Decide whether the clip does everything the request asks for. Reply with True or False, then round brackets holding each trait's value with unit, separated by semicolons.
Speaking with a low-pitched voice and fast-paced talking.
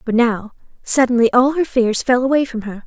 False (245 Hz; 210 wpm)